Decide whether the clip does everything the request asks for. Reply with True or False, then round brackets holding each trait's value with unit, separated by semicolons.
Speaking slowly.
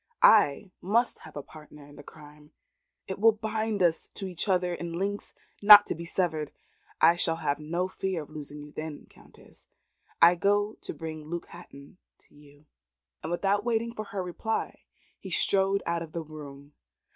False (180 wpm)